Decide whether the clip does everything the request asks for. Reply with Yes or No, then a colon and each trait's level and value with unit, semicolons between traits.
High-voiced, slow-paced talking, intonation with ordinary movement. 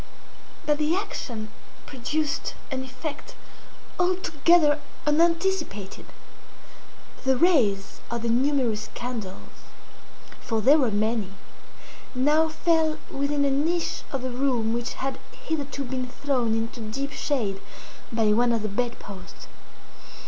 Yes: very high, 260 Hz; slow, 120 wpm; average, 4.6 semitones